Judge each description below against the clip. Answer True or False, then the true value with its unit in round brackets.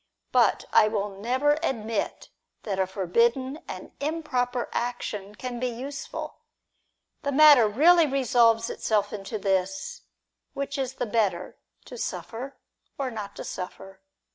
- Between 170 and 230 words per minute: False (135 wpm)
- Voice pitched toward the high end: True (235 Hz)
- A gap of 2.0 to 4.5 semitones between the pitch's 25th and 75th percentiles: False (4.9 semitones)